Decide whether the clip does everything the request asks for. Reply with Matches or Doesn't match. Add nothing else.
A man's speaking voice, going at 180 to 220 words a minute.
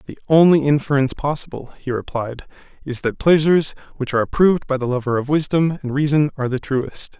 Matches